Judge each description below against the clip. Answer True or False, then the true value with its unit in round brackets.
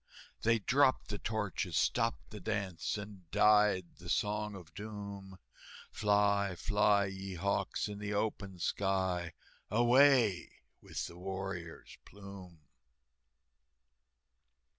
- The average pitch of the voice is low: True (100 Hz)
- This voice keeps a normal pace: False (105 wpm)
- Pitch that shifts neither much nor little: False (2.0 semitones)